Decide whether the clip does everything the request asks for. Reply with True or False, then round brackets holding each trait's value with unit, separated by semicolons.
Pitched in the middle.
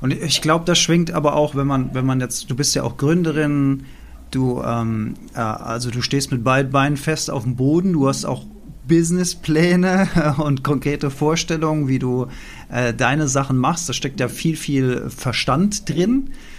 True (145 Hz)